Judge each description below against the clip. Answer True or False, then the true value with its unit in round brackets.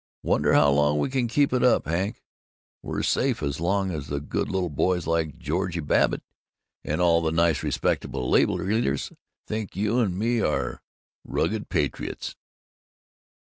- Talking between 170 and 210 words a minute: False (155 wpm)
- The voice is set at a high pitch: False (90 Hz)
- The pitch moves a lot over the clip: True (6.0 semitones)